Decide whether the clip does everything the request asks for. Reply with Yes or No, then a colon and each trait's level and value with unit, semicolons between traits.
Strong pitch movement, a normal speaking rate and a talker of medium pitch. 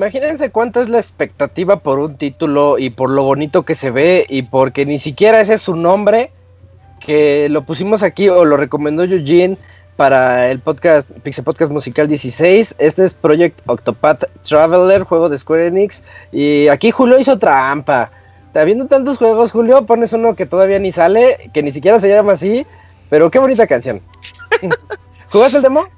Yes: wide, 7.1 semitones; average, 175 wpm; medium, 175 Hz